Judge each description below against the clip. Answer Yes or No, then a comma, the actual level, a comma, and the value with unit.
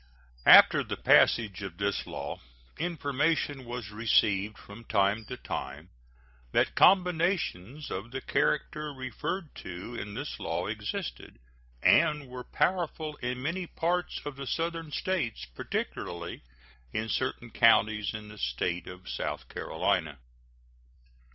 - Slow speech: Yes, slow, 125 wpm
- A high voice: No, low, 120 Hz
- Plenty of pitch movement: Yes, wide, 7.2 semitones